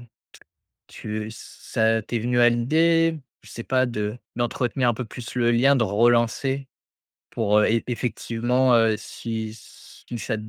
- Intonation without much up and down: Yes, narrow, 1.9 semitones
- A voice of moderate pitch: No, low, 120 Hz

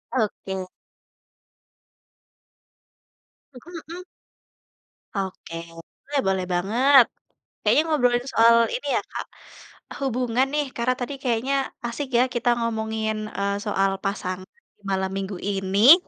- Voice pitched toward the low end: No, high, 230 Hz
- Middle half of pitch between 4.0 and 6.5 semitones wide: Yes, average, 4.8 semitones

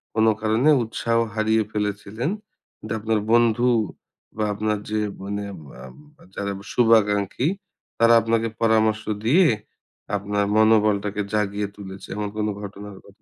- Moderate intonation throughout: No, narrow, 1.6 semitones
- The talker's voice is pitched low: Yes, low, 110 Hz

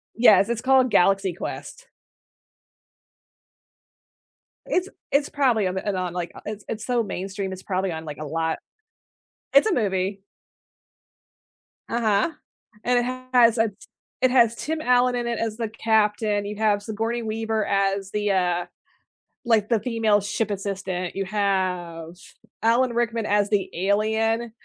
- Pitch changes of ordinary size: Yes, average, 3.2 semitones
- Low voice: No, high, 215 Hz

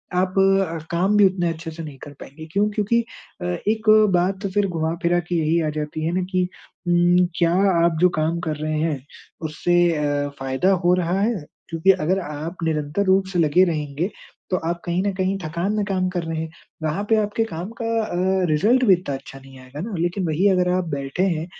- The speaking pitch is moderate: Yes, medium, 175 Hz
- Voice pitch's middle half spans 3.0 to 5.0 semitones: Yes, average, 3.3 semitones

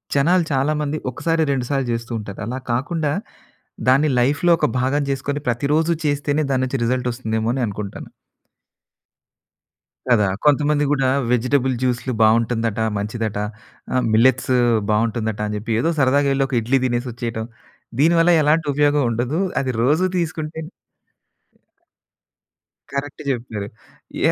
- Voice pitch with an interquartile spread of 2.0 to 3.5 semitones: No, average, 4.0 semitones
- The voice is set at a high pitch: No, low, 130 Hz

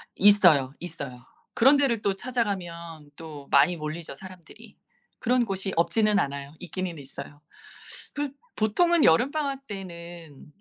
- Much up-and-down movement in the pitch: Yes, wide, 6.2 semitones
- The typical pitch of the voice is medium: Yes, medium, 180 Hz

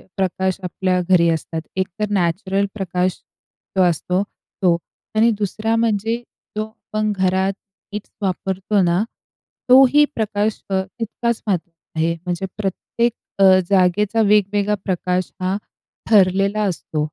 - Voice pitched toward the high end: Yes, high, 195 Hz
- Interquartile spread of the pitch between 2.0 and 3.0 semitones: Yes, narrow, 2.6 semitones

